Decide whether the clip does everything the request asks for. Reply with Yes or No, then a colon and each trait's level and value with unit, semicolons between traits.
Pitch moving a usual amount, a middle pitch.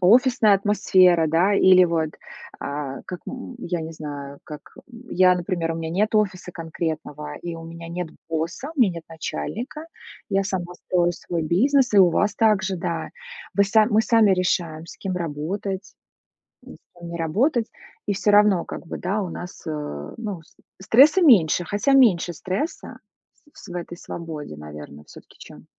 Yes: average, 4.0 semitones; medium, 180 Hz